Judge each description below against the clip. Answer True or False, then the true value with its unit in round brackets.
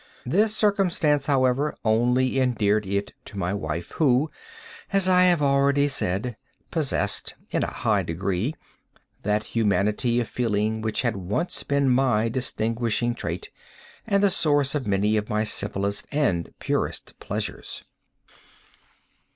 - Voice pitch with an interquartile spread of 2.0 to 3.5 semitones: False (5.4 semitones)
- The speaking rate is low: True (130 wpm)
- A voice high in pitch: False (120 Hz)